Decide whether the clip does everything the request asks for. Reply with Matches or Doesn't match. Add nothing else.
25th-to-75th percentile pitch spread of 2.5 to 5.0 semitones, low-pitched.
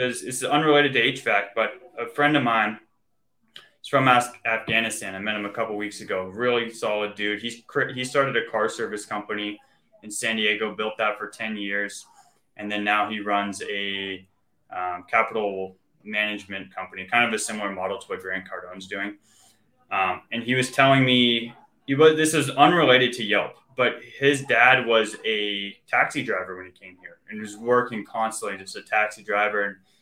Matches